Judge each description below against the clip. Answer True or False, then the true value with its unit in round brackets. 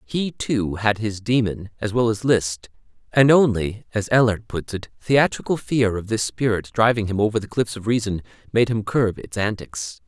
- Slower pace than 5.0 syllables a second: True (4.8 syllables/s)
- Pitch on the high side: False (105 Hz)